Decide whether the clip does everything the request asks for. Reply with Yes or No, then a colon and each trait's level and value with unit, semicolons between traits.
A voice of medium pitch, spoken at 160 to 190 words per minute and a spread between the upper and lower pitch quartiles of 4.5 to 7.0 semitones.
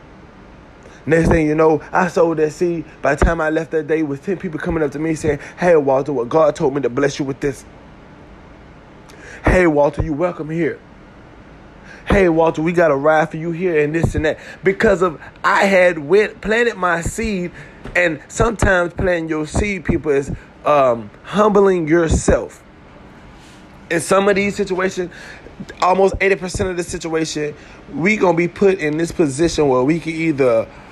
No: medium, 165 Hz; average, 180 wpm; average, 3.2 semitones